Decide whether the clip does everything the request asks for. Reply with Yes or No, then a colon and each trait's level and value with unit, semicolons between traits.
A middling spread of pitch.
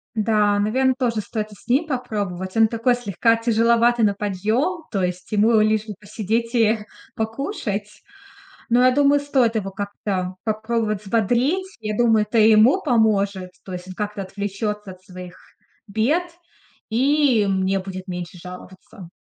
Yes: average, 3.0 semitones